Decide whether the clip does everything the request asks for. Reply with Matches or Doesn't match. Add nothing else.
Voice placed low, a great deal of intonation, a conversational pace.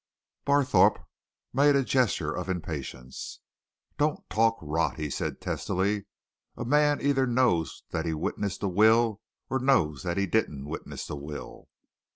Matches